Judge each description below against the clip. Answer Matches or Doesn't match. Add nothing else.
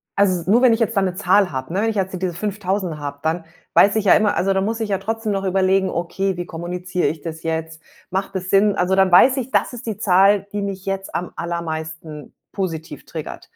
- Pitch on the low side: Doesn't match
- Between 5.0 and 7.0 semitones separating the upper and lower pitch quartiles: Doesn't match